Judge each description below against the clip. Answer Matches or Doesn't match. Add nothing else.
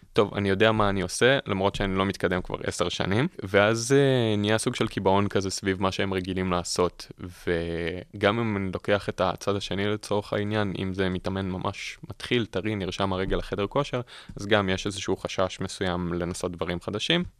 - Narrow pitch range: Matches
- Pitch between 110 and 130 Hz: Doesn't match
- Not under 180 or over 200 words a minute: Matches